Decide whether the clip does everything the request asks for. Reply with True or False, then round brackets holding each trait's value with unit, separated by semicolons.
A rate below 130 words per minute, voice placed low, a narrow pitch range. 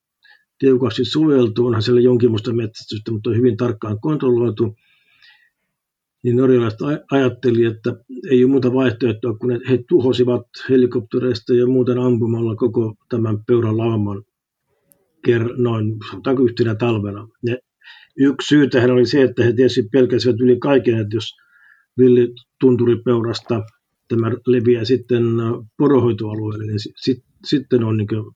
True (120 wpm; 120 Hz; 1.7 semitones)